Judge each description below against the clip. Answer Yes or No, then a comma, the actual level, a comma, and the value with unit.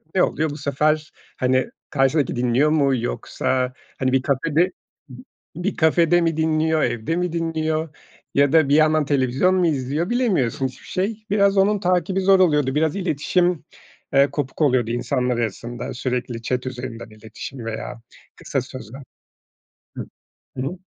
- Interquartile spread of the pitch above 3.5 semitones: Yes, average, 4.5 semitones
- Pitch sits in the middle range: Yes, medium, 145 Hz